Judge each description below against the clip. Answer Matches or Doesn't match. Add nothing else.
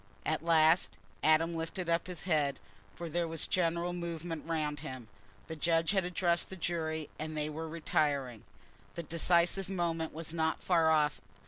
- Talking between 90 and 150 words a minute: Doesn't match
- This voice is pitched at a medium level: Matches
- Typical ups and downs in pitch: Doesn't match